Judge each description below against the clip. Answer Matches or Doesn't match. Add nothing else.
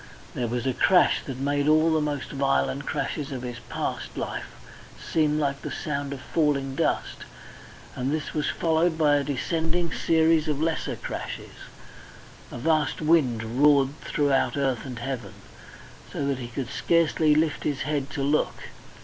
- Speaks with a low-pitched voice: Doesn't match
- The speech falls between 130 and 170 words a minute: Matches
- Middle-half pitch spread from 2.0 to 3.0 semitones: Matches